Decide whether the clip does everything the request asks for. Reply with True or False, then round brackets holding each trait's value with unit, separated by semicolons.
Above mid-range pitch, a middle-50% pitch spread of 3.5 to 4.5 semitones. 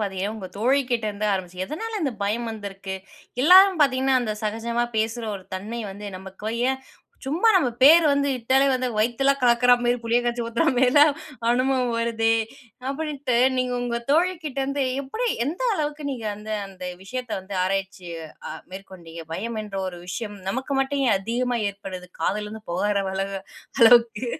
False (235 Hz; 5.0 semitones)